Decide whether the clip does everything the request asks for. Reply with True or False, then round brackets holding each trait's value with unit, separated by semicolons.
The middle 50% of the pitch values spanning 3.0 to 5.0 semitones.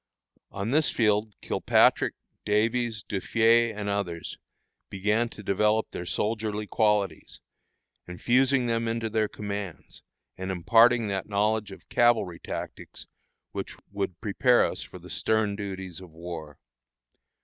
False (2.6 semitones)